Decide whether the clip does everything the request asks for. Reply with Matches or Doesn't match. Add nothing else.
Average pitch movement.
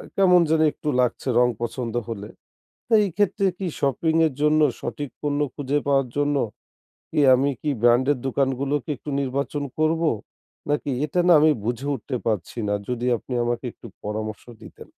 Matches